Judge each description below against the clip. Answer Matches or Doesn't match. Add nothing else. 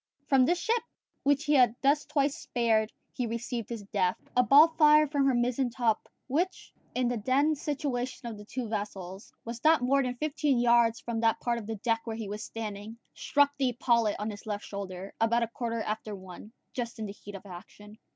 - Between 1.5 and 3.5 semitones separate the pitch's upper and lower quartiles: Doesn't match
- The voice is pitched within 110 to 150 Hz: Doesn't match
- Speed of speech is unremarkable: Doesn't match